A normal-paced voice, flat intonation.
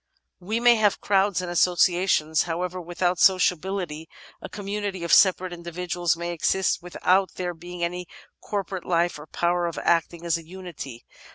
Yes: average, 160 wpm; narrow, 1.7 semitones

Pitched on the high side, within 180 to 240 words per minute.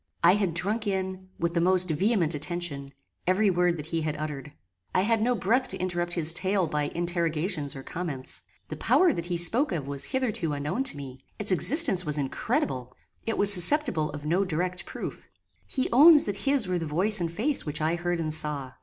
No: medium, 175 Hz; average, 200 wpm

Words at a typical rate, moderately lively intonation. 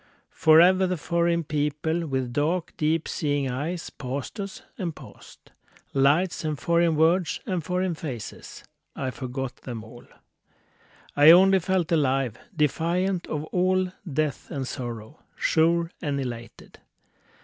No: slow, 125 wpm; average, 4.2 semitones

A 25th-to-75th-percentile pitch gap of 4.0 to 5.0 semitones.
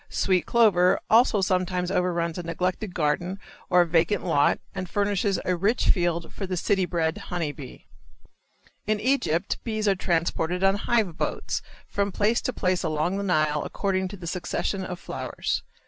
No: average, 2.8 semitones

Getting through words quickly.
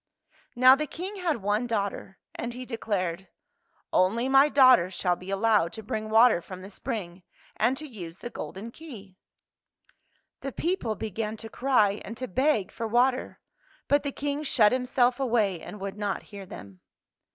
No: average, 175 wpm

